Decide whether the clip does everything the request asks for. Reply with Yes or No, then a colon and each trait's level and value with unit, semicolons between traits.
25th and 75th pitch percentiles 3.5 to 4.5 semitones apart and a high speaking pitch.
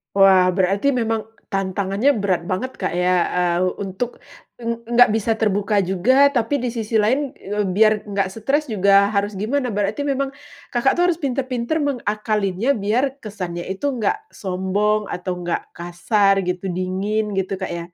Yes: average, 4.2 semitones; high, 210 Hz